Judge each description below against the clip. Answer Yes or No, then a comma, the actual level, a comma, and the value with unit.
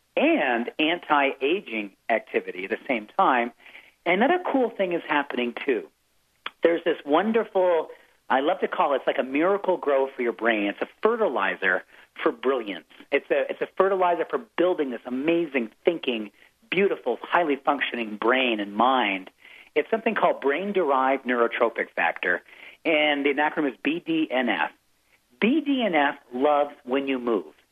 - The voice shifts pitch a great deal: Yes, wide, 8.3 semitones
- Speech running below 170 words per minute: Yes, average, 145 wpm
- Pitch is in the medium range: Yes, medium, 150 Hz